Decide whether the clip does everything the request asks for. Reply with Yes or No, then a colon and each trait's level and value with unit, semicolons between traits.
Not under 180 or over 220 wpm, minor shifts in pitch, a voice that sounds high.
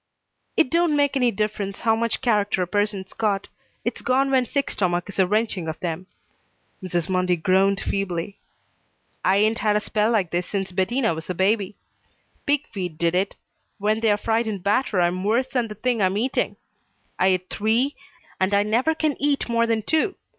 No: average, 190 wpm; average, 3.8 semitones; high, 210 Hz